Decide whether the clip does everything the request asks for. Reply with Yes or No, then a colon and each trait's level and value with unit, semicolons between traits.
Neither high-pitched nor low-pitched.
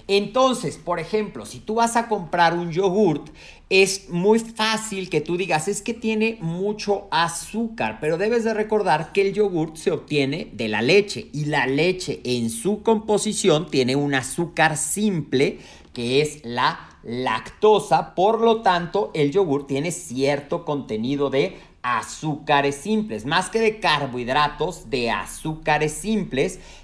Yes: medium, 170 Hz